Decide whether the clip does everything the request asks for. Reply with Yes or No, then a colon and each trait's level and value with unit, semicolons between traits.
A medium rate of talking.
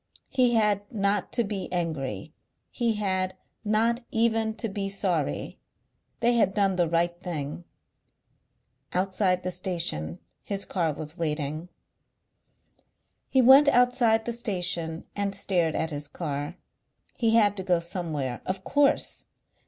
No: slow, 130 wpm